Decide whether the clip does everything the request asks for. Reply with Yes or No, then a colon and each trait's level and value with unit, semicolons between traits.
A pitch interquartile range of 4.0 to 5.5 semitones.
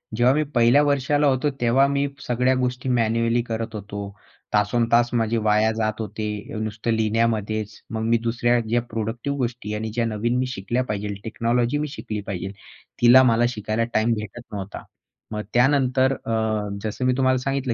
No: average, 2.7 semitones